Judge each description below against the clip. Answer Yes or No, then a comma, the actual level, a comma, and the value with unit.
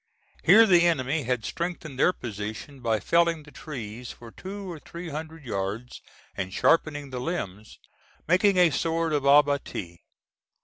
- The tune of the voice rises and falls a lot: Yes, wide, 6.0 semitones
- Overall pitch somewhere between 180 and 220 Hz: No, medium, 145 Hz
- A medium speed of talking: Yes, average, 145 wpm